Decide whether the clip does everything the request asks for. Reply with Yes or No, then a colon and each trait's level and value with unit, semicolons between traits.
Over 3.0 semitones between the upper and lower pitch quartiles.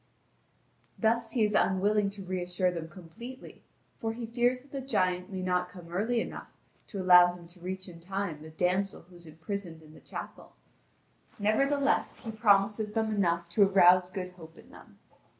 Yes: average, 3.5 semitones